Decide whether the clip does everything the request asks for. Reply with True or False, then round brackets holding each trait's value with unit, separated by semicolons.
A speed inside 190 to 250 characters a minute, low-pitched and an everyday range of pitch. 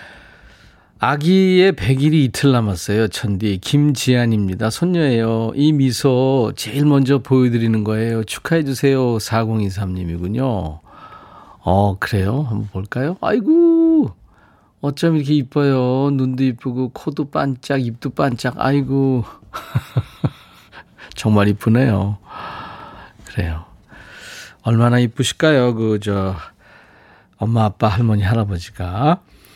True (235 characters per minute; 120 Hz; 4.5 semitones)